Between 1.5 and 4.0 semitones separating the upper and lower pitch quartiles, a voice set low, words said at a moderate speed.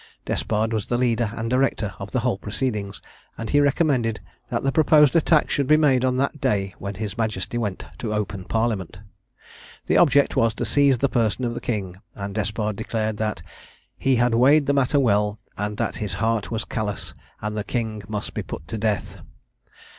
Yes: average, 3.7 semitones; low, 115 Hz; average, 190 wpm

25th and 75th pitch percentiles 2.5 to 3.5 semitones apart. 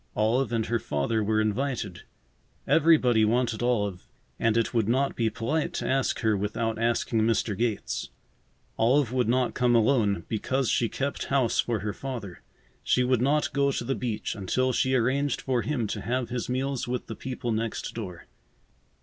Yes: average, 2.9 semitones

